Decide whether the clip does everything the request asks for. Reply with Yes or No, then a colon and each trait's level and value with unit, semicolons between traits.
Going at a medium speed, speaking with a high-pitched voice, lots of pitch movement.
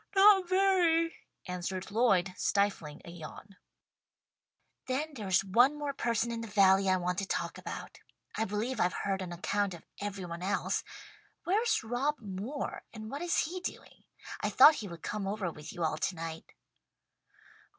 Yes: average, 160 wpm; high, 205 Hz; wide, 7.0 semitones